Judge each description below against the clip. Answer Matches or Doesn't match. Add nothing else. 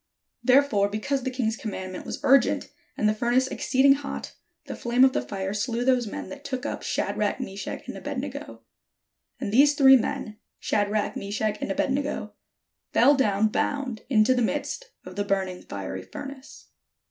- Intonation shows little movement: Doesn't match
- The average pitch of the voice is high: Matches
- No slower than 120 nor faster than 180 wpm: Matches